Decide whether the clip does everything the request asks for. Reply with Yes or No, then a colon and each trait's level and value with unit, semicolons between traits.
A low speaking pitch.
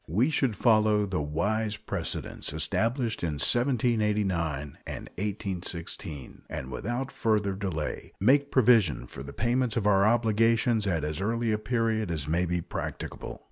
Yes: low, 105 Hz